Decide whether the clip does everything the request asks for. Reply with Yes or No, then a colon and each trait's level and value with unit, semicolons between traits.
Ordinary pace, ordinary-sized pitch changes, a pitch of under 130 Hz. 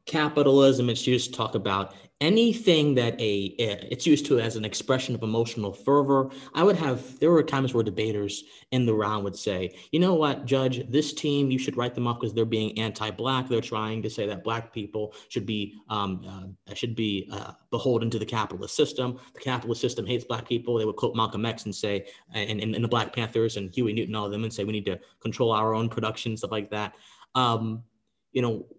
No: fast, 210 wpm; average, 3.2 semitones; low, 115 Hz